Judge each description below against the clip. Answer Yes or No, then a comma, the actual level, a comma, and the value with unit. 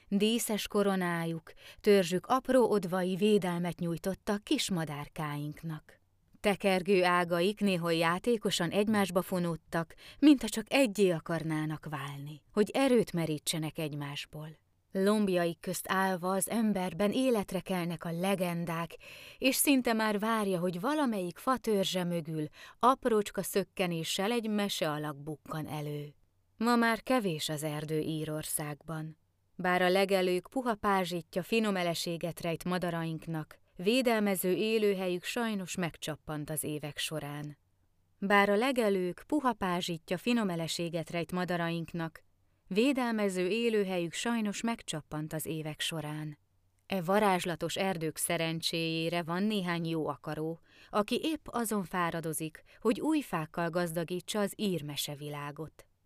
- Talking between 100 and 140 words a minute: Yes, average, 110 wpm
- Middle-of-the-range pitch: Yes, medium, 180 Hz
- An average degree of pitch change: Yes, average, 4.5 semitones